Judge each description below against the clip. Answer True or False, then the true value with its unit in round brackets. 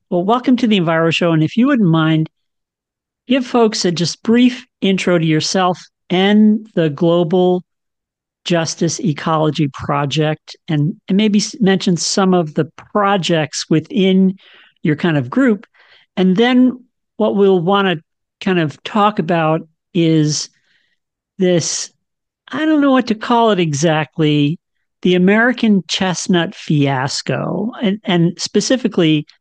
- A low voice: False (180 Hz)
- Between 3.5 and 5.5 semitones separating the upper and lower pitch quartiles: True (4.8 semitones)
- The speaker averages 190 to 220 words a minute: False (135 wpm)